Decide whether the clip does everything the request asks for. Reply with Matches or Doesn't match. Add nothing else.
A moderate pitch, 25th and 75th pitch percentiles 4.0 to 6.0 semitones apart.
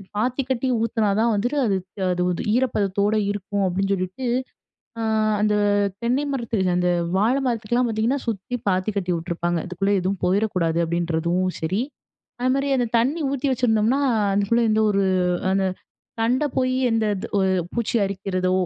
Doesn't match